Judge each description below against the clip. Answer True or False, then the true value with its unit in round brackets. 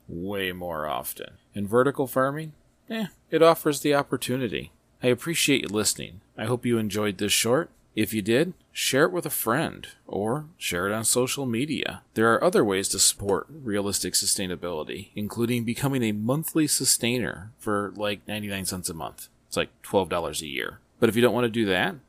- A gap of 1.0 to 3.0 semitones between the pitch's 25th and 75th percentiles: False (4.7 semitones)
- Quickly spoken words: False (180 wpm)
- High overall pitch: False (115 Hz)